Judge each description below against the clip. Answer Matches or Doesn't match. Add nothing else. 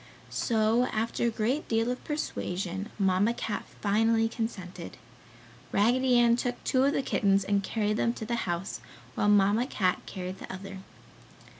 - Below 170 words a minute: Matches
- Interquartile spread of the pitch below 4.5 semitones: Matches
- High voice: Matches